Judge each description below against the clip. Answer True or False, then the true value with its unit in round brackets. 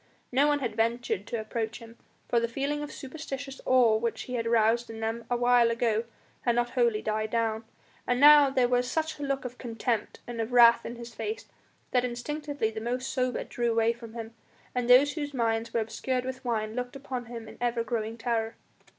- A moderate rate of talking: False (210 wpm)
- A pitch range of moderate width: False (2.1 semitones)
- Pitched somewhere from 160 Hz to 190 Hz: False (240 Hz)